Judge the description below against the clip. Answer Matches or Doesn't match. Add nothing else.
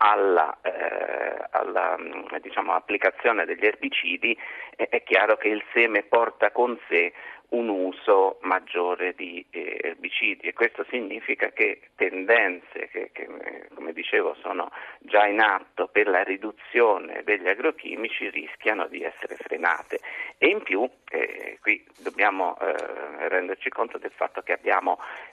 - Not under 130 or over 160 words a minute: Matches